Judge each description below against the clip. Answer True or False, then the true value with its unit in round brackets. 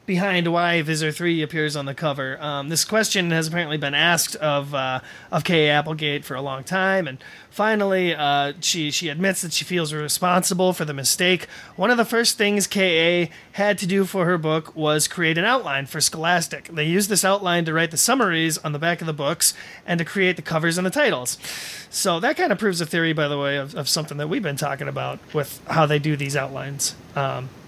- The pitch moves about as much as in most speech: True (3.6 semitones)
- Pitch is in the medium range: True (165 Hz)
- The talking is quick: True (220 wpm)